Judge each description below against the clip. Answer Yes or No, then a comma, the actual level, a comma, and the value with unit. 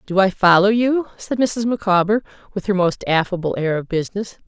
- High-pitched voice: Yes, high, 195 Hz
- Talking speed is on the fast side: No, average, 190 wpm